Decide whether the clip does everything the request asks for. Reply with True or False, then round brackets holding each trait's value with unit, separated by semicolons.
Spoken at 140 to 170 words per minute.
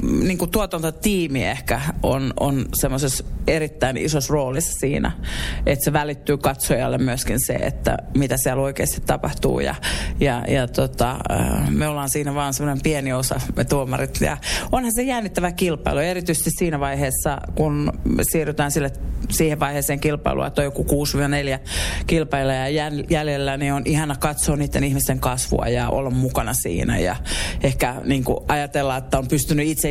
True (150 wpm)